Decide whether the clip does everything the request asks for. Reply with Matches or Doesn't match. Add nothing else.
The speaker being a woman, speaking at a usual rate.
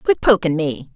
Matches